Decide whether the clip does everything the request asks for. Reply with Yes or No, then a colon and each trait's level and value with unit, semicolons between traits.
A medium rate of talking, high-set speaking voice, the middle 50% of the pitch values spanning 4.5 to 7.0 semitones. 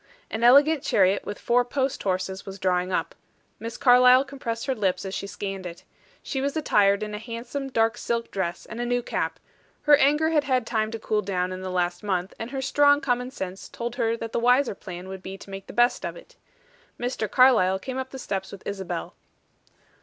No: fast, 215 wpm; high, 225 Hz; average, 5.1 semitones